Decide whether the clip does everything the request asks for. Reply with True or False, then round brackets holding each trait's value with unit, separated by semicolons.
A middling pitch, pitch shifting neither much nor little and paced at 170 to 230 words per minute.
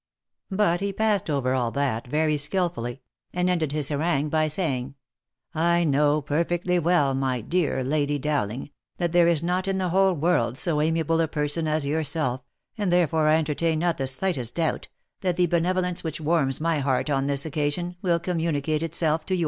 True (155 Hz; 3.4 semitones; 190 wpm)